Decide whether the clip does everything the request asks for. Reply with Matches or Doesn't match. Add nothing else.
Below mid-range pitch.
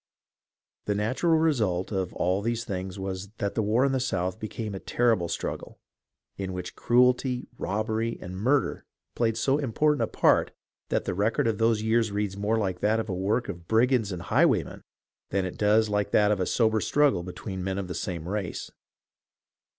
Matches